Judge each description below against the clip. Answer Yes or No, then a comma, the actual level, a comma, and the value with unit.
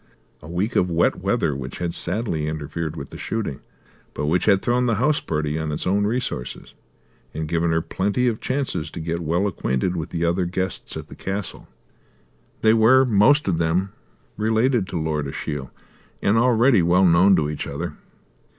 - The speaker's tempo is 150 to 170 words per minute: No, average, 180 wpm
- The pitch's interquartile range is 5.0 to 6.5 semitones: Yes, wide, 5.5 semitones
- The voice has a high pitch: No, very low, 90 Hz